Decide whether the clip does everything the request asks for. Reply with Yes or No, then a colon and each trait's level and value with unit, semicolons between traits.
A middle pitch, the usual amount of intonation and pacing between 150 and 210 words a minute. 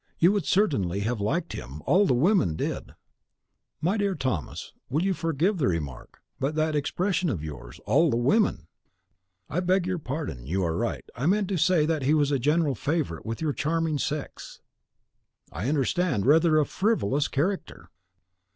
No: medium, 150 Hz; wide, 7.8 semitones; average, 175 wpm